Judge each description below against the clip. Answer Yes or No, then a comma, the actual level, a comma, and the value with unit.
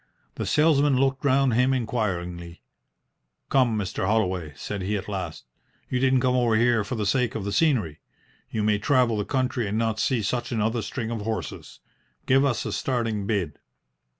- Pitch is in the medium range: No, low, 115 Hz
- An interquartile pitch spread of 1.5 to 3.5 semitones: No, average, 3.9 semitones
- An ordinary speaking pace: Yes, average, 180 wpm